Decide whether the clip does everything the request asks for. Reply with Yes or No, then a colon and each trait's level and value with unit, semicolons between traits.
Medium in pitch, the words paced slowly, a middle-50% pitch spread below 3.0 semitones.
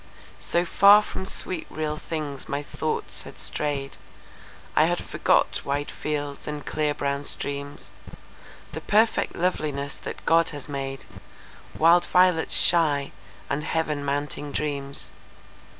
Yes: medium, 150 Hz; slow, 115 wpm; narrow, 2.5 semitones